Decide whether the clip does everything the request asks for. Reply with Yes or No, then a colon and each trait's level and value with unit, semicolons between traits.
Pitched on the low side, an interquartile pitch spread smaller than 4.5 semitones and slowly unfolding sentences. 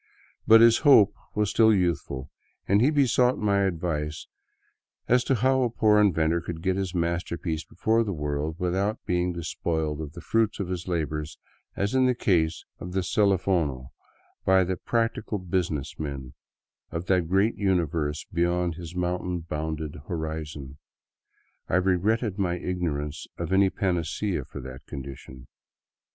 No: very low, 90 Hz; average, 4.1 semitones; average, 155 wpm